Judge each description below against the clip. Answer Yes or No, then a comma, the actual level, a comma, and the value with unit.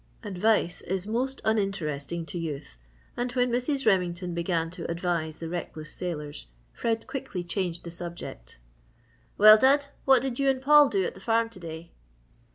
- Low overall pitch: No, medium, 185 Hz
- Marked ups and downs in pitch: Yes, wide, 5.9 semitones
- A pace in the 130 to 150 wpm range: No, average, 165 wpm